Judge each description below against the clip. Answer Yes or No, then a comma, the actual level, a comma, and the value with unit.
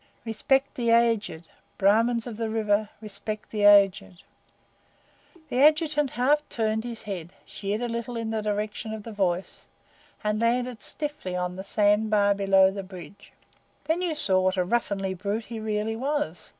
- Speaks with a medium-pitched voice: No, high, 215 Hz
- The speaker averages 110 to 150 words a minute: No, average, 165 wpm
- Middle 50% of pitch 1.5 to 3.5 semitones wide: Yes, average, 2.9 semitones